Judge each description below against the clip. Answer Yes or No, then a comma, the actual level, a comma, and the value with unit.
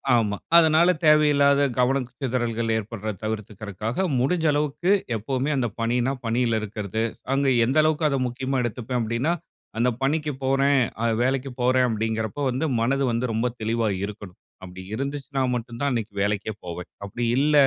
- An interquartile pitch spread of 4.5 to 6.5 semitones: No, average, 3.9 semitones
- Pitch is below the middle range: Yes, low, 125 Hz